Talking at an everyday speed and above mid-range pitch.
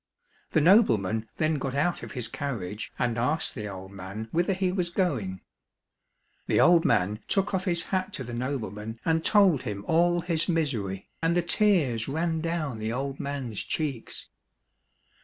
No: average, 165 wpm; medium, 140 Hz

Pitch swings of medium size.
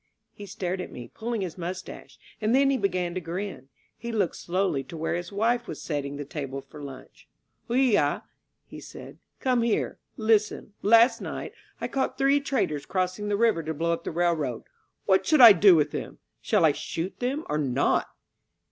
No: wide, 5.9 semitones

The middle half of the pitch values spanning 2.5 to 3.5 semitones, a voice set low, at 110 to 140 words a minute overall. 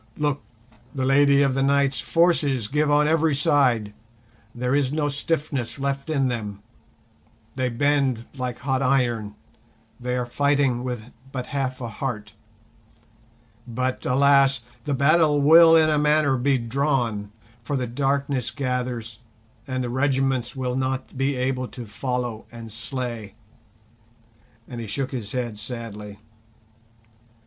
Yes: average, 3.0 semitones; low, 130 Hz; slow, 135 wpm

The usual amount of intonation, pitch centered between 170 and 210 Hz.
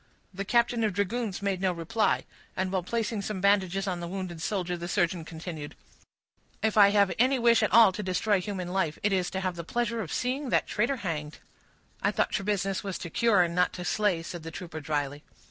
Yes: average, 3.4 semitones; high, 190 Hz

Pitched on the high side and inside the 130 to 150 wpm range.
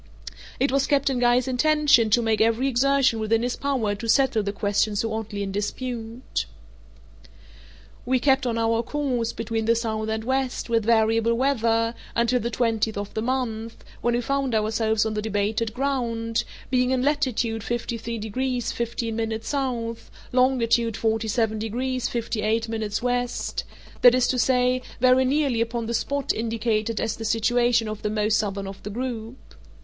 No: high, 230 Hz; average, 160 wpm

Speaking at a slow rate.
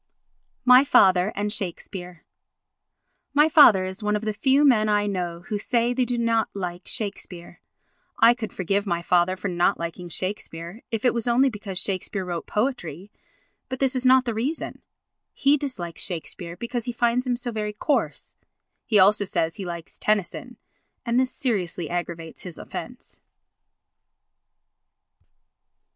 No: average, 155 wpm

